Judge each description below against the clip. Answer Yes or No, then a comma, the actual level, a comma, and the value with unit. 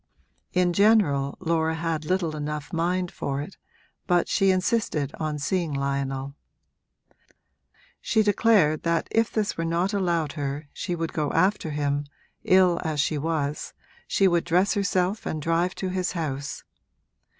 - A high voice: No, medium, 165 Hz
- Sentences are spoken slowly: No, average, 145 wpm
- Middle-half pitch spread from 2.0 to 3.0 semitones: No, average, 3.7 semitones